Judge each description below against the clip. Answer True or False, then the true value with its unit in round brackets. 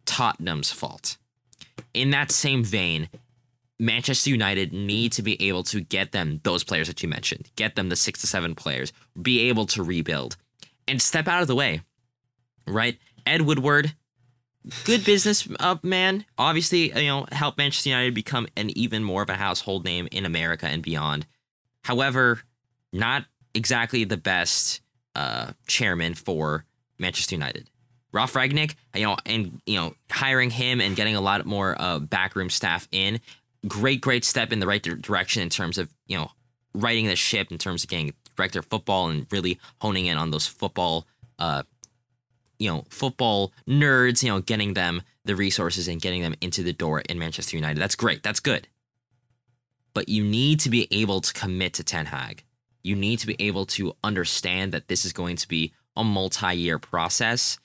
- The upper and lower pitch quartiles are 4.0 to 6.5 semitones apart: True (5.3 semitones)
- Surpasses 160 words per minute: True (175 wpm)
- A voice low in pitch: True (110 Hz)